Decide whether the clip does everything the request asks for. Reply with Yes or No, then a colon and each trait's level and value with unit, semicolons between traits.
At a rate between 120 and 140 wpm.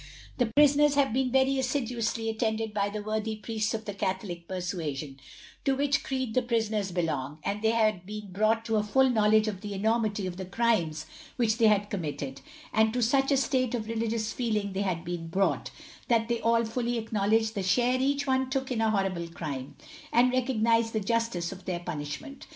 No: average, 195 wpm